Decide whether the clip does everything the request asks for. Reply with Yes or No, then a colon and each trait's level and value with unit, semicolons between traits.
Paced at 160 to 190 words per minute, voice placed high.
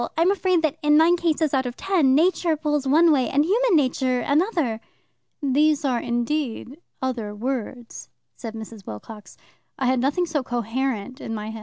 Yes: average, 170 wpm; very high, 270 Hz